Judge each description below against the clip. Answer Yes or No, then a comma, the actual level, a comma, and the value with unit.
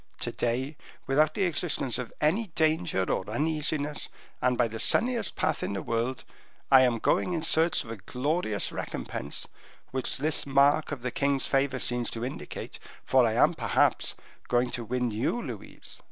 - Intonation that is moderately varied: Yes, average, 4.3 semitones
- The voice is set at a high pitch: No, low, 135 Hz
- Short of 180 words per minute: Yes, average, 170 wpm